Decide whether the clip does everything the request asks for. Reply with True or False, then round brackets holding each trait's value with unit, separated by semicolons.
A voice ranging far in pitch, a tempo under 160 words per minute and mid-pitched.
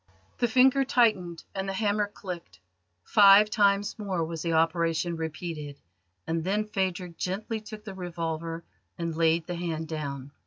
False (3.8 semitones; 150 wpm; 175 Hz)